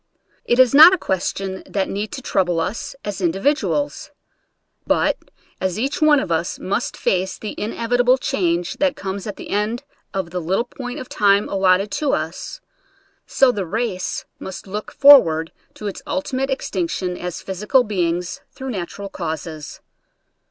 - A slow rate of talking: No, average, 160 wpm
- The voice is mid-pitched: No, high, 200 Hz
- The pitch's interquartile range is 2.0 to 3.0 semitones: No, wide, 5.6 semitones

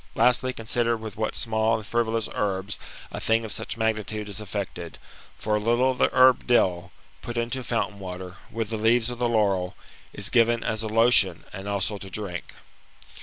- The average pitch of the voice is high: No, low, 110 Hz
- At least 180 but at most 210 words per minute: Yes, average, 185 wpm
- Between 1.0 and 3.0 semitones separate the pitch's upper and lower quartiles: Yes, average, 2.7 semitones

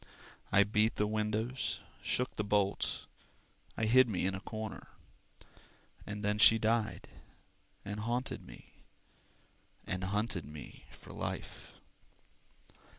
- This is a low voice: Yes, low, 105 Hz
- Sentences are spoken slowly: Yes, slow, 115 wpm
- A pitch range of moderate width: No, narrow, 1.7 semitones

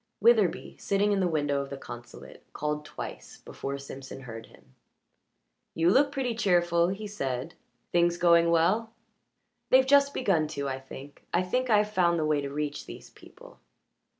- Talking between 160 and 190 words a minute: Yes, average, 165 wpm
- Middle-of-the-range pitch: Yes, medium, 170 Hz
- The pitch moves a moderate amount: No, wide, 6.5 semitones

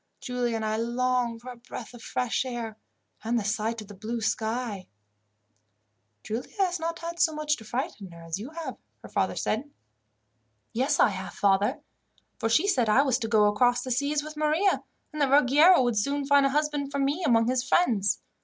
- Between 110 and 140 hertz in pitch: No, very high, 250 Hz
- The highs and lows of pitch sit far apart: No, average, 4.6 semitones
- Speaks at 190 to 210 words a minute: Yes, average, 200 wpm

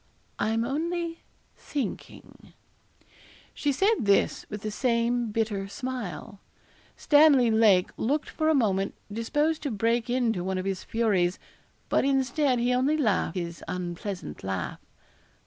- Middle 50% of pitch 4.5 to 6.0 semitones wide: Yes, wide, 5.5 semitones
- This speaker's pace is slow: Yes, slow, 130 wpm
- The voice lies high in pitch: Yes, high, 230 Hz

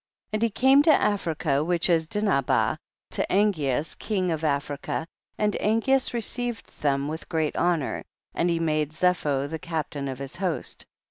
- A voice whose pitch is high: No, medium, 165 Hz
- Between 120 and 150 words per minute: No, average, 165 wpm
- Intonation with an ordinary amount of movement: No, wide, 5.7 semitones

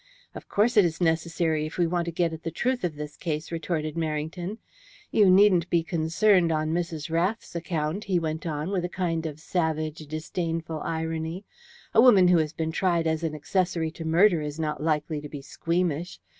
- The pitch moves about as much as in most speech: No, narrow, 2.2 semitones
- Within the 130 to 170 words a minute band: No, average, 195 wpm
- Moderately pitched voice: Yes, medium, 165 Hz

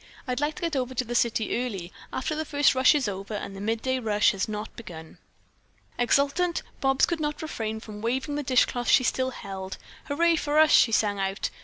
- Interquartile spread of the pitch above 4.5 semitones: Yes, wide, 5.5 semitones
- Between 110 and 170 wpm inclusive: No, fast, 205 wpm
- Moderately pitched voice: No, very high, 250 Hz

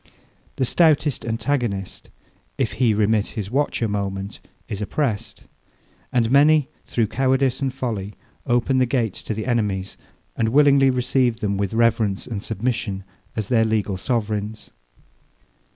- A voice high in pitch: No, low, 115 Hz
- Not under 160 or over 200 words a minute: No, slow, 135 wpm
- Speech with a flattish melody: No, average, 3.9 semitones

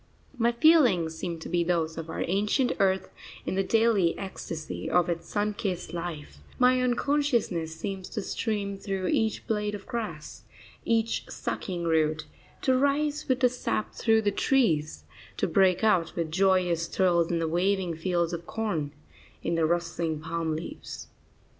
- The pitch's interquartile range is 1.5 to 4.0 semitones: No, average, 5.0 semitones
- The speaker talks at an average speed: Yes, average, 160 wpm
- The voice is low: No, medium, 185 Hz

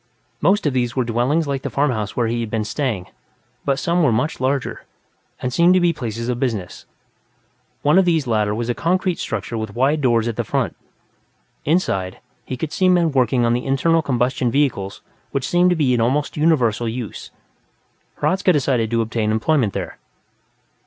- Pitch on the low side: Yes, low, 130 Hz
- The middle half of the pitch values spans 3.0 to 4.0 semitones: No, average, 4.9 semitones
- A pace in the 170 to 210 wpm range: Yes, average, 185 wpm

